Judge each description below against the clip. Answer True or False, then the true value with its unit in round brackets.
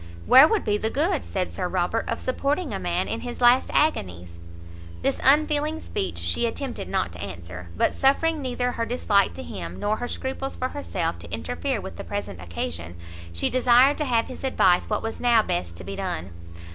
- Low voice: False (225 Hz)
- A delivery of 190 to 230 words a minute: True (195 wpm)